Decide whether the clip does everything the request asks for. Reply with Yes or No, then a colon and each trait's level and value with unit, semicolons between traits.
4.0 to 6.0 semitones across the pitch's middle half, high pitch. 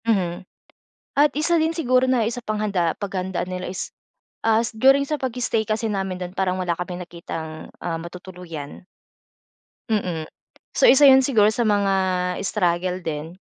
Yes: average, 4.8 semitones; high, 195 Hz